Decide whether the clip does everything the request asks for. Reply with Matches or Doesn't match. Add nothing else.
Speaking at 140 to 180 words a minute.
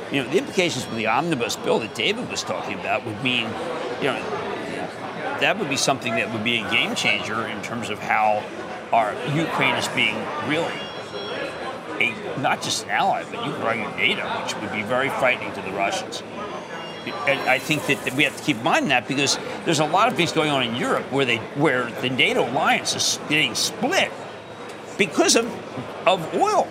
Doesn't match